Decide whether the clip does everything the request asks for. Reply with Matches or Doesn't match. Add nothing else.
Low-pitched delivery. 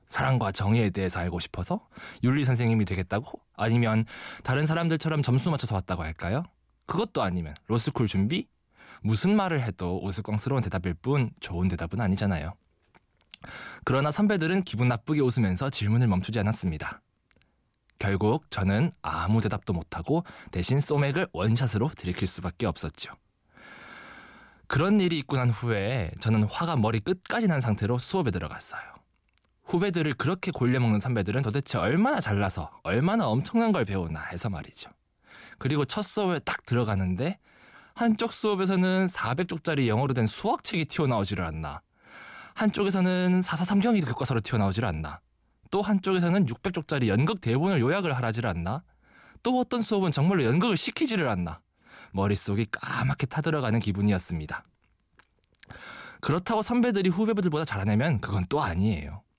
Matches